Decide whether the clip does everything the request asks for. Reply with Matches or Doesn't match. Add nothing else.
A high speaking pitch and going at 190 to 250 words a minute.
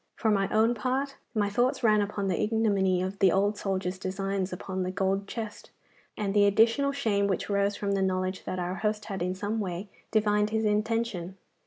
Matches